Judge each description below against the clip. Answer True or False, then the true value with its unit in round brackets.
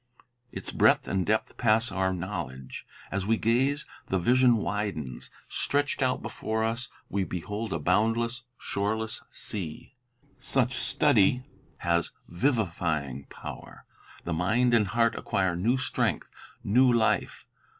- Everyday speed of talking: False (125 wpm)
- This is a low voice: True (110 Hz)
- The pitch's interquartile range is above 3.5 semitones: True (4.5 semitones)